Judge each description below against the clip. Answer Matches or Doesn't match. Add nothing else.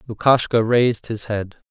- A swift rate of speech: Doesn't match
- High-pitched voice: Doesn't match